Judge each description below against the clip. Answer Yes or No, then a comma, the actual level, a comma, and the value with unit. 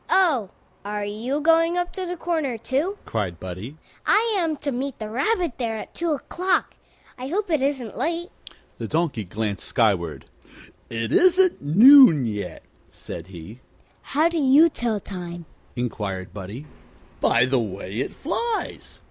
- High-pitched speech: Yes, high, 235 Hz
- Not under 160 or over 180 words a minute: No, average, 150 wpm